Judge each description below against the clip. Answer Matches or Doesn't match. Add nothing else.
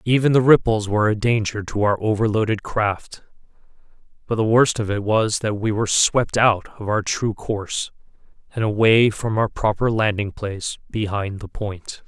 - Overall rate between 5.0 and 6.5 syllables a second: Doesn't match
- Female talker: Doesn't match